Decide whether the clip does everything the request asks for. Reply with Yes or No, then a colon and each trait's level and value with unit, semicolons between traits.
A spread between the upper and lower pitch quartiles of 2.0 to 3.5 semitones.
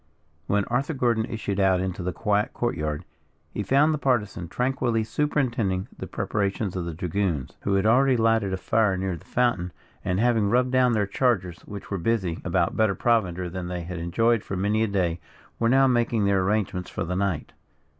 No: average, 4.3 semitones